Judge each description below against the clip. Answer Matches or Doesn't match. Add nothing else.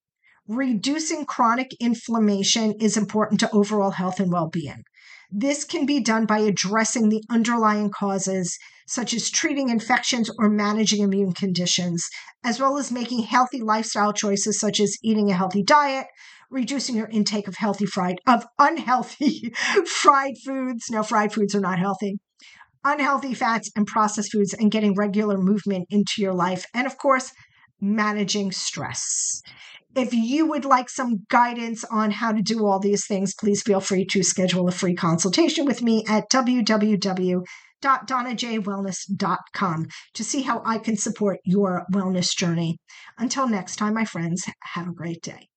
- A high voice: Matches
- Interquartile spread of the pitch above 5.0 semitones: Doesn't match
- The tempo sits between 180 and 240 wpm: Doesn't match